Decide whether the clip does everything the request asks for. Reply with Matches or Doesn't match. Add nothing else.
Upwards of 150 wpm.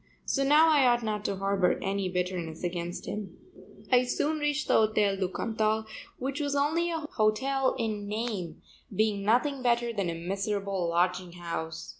Matches